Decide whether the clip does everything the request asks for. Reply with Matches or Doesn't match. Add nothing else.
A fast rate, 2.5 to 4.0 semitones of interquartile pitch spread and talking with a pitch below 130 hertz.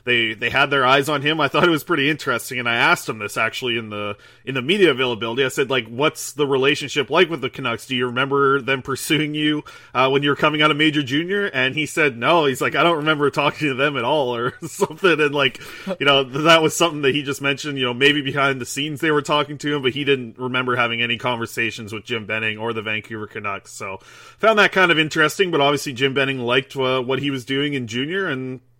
Doesn't match